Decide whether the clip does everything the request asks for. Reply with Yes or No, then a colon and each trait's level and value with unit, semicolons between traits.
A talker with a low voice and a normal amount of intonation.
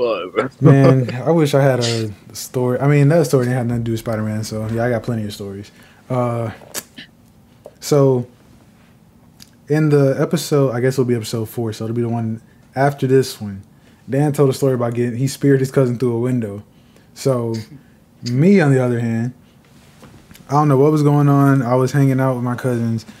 Yes: low, 125 Hz; average, 3.0 semitones